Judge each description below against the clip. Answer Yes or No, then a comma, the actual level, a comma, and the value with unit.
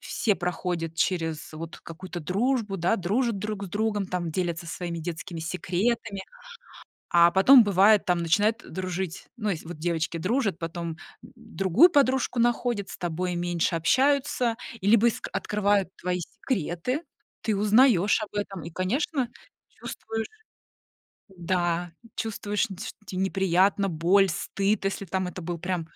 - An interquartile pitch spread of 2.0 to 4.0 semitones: Yes, average, 3.7 semitones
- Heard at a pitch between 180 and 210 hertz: Yes, high, 190 Hz